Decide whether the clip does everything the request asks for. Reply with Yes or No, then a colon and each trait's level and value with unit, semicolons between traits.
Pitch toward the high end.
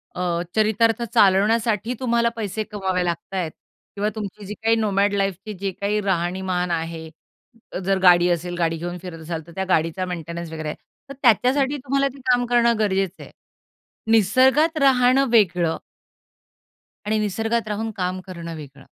Yes: high, 195 Hz